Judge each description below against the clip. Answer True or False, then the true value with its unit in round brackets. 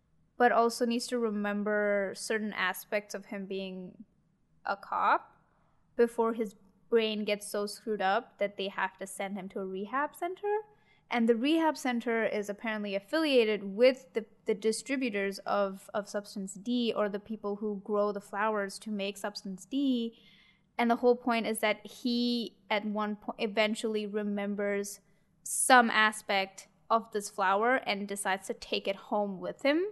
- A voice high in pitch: True (210 Hz)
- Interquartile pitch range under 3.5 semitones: True (2.8 semitones)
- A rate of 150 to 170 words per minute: True (160 wpm)